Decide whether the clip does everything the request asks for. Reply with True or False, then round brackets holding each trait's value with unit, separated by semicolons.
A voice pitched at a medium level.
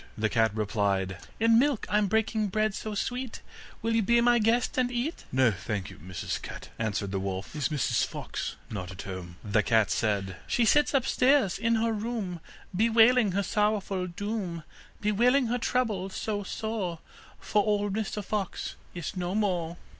False (205 Hz)